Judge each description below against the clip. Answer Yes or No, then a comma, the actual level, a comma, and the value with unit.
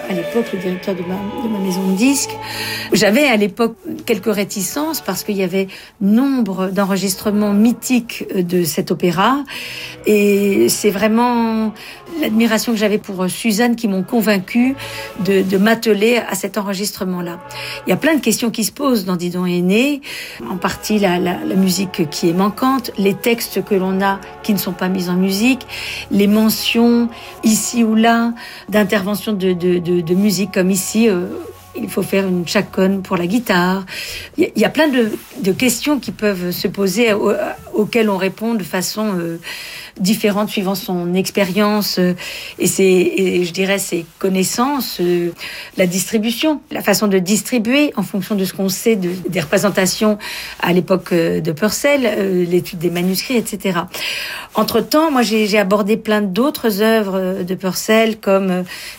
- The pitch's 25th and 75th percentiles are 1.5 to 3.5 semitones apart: Yes, average, 3.2 semitones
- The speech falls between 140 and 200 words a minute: Yes, average, 170 wpm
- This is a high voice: Yes, high, 205 Hz